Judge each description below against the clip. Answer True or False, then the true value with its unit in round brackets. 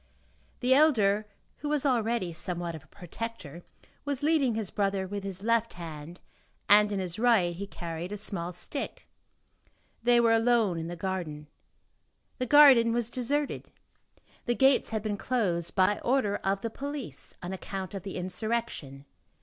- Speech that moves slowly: False (160 wpm)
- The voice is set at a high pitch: True (205 Hz)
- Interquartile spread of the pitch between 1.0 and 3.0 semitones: False (5.0 semitones)